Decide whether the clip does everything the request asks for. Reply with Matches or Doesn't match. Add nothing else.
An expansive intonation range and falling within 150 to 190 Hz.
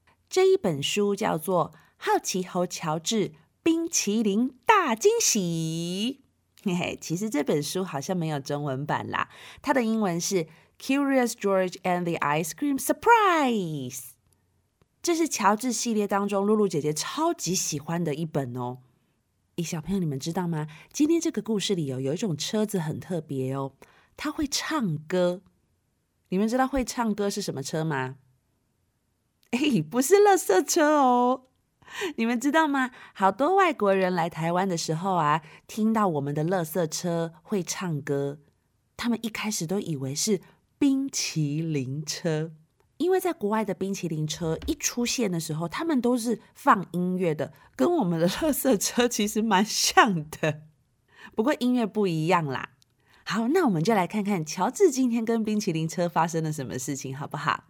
Matches